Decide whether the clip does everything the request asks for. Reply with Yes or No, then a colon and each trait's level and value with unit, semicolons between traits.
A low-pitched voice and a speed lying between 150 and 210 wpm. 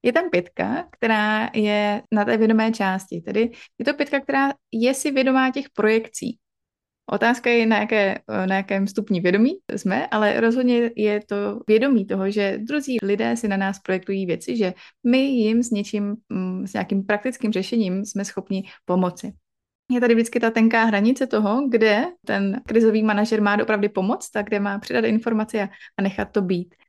No: high, 215 Hz; fast, 170 wpm